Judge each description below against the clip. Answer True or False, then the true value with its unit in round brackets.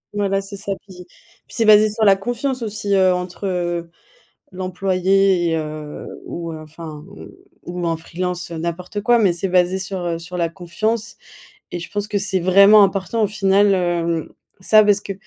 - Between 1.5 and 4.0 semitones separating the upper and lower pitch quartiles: True (2.8 semitones)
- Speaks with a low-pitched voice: False (190 Hz)